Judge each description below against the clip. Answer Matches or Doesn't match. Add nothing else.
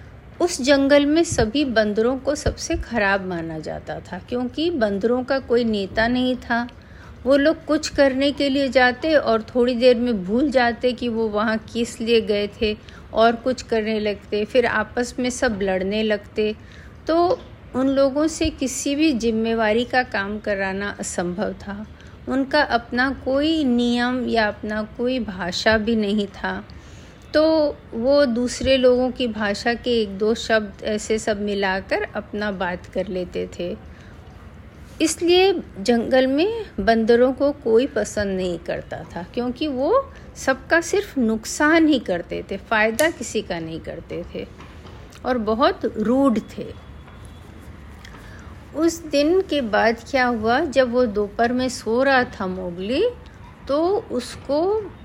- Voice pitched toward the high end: Matches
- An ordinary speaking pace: Matches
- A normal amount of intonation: Matches